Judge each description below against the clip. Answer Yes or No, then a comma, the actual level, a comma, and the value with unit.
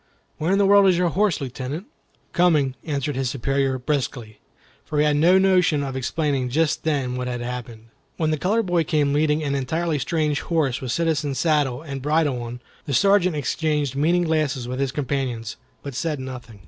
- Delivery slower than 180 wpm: No, average, 185 wpm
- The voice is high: No, medium, 145 Hz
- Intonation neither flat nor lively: Yes, average, 3.8 semitones